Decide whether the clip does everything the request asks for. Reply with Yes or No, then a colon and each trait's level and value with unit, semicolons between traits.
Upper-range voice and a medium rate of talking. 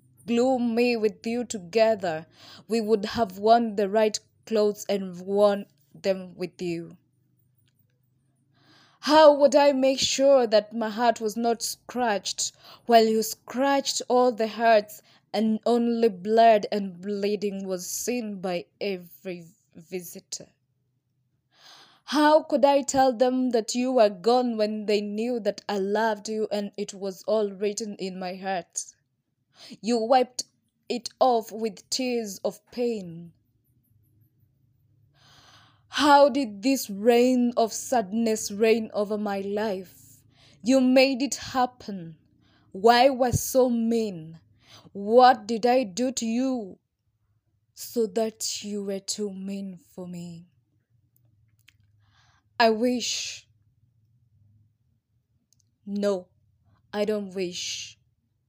No: high, 205 Hz; slow, 120 wpm